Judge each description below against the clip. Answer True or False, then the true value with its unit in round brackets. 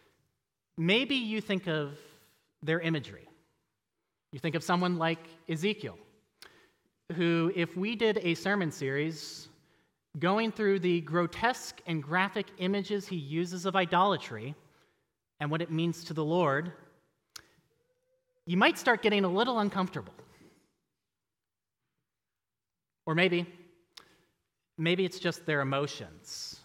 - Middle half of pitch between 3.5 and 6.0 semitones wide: True (3.8 semitones)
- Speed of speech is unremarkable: False (115 wpm)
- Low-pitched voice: False (175 Hz)